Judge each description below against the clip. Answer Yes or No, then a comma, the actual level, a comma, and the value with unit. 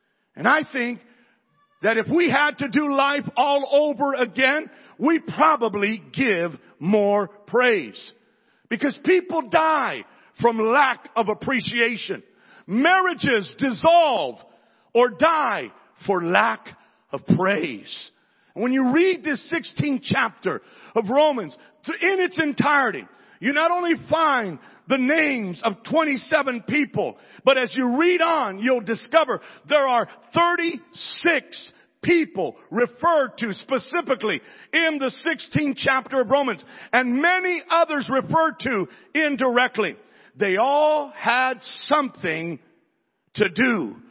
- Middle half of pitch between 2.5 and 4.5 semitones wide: No, average, 4.9 semitones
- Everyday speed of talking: No, slow, 115 wpm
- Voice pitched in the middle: No, very high, 270 Hz